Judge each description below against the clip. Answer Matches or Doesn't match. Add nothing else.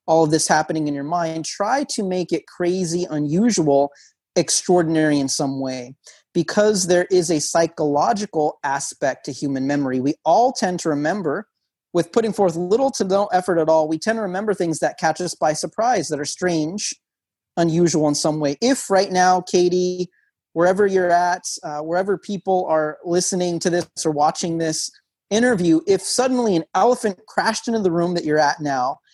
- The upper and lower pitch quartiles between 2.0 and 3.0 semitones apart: Doesn't match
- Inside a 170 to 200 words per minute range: Matches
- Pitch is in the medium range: Matches